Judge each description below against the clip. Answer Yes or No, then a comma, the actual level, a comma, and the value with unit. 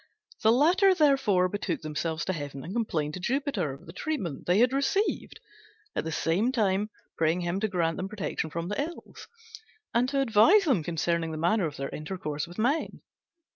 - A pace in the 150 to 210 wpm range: Yes, average, 185 wpm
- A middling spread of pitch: No, wide, 7.5 semitones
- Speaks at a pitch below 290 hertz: Yes, high, 190 Hz